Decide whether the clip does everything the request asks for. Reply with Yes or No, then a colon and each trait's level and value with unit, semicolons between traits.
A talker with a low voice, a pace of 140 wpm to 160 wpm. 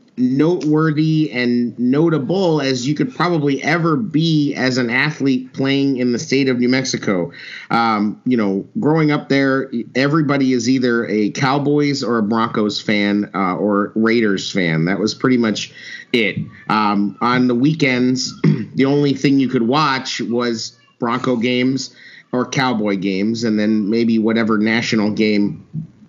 Yes: low, 125 Hz; average, 150 wpm